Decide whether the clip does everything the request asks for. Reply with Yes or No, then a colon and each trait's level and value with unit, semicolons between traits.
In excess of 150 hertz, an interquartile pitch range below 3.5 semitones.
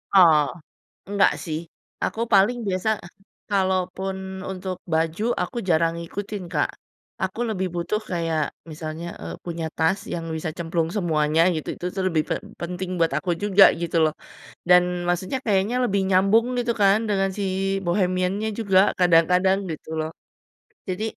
Yes: medium, 185 Hz; average, 2.9 semitones